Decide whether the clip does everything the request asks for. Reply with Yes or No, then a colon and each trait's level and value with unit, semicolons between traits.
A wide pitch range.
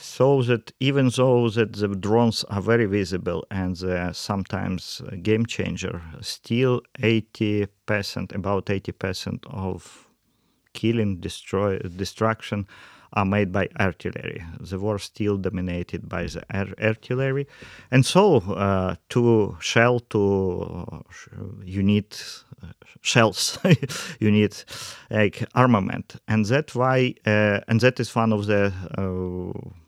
No: average, 3.3 semitones